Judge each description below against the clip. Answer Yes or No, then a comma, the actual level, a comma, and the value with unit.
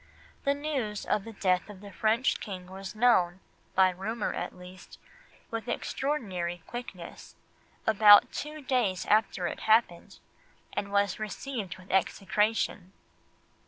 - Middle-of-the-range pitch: No, high, 205 Hz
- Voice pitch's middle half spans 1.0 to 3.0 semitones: No, average, 3.6 semitones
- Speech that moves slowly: Yes, slow, 125 wpm